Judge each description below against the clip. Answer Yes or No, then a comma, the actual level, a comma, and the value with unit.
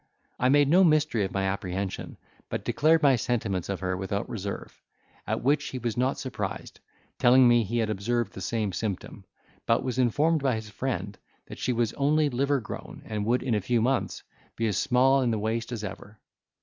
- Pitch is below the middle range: Yes, low, 115 Hz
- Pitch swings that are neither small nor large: Yes, average, 4.2 semitones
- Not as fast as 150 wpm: No, average, 190 wpm